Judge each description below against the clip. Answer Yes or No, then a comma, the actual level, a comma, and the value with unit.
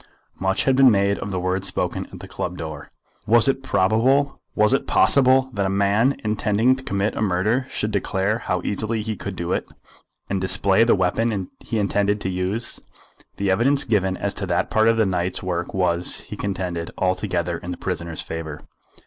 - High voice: No, low, 100 Hz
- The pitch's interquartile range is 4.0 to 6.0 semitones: No, average, 3.5 semitones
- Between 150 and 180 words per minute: No, average, 190 wpm